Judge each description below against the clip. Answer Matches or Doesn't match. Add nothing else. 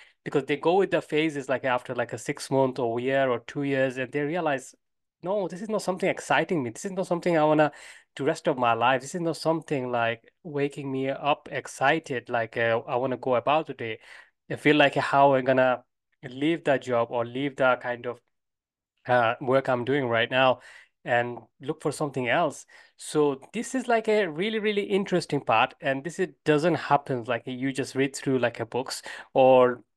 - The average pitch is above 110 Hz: Matches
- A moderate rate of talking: Doesn't match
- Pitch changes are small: Doesn't match